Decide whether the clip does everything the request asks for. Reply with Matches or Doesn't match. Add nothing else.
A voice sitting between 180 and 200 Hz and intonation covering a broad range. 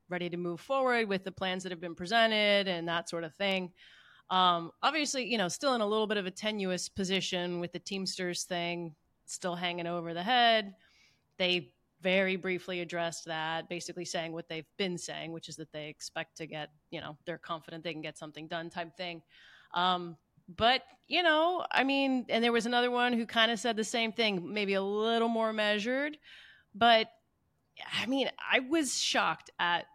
Doesn't match